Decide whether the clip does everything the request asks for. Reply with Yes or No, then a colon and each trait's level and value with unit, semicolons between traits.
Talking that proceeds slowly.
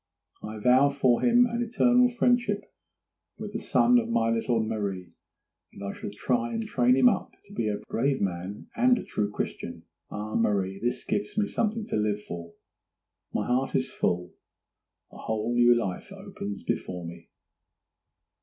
No: average, 165 wpm